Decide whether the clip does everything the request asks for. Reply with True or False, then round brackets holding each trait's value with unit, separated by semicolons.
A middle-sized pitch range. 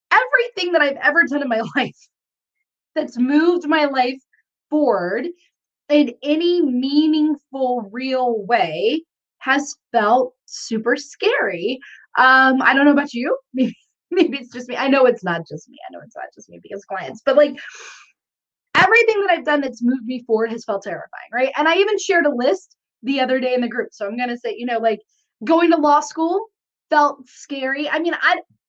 True (4.5 semitones)